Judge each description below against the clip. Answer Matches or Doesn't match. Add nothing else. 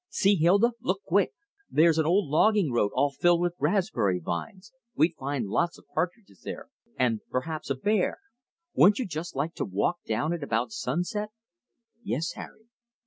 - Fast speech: Doesn't match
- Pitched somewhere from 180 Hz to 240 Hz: Doesn't match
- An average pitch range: Doesn't match